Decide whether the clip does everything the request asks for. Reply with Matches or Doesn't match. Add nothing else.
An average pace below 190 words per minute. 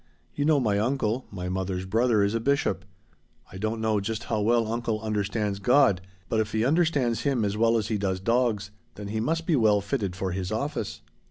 Doesn't match